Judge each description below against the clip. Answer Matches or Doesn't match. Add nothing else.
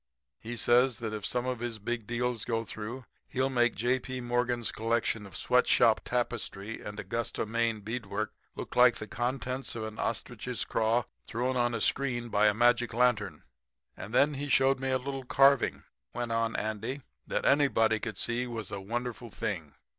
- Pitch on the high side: Doesn't match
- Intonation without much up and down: Matches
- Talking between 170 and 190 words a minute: Matches